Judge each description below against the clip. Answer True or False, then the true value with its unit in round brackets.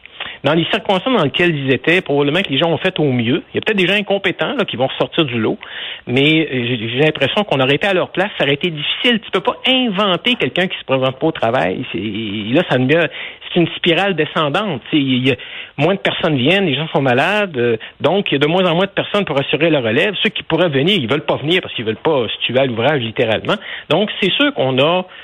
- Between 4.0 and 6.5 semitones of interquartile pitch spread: True (5.6 semitones)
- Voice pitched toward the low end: False (160 Hz)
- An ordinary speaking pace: False (260 wpm)